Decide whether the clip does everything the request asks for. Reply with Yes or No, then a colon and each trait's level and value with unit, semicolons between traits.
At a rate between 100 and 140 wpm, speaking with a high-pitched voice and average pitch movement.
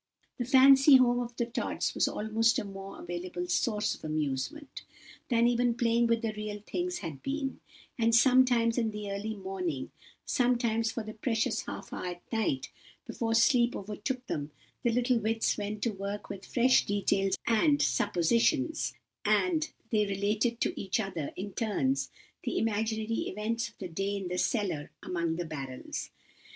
No: average, 165 wpm; high, 220 Hz; average, 3.6 semitones